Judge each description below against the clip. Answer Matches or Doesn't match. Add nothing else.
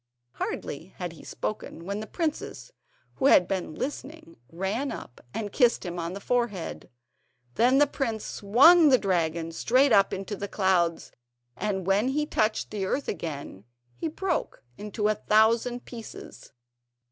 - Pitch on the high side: Matches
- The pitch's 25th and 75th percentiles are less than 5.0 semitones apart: Doesn't match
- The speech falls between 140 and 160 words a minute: Matches